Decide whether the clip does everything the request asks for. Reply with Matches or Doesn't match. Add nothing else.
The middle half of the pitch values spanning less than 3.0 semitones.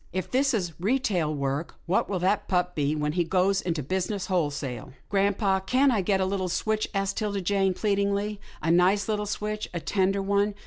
Matches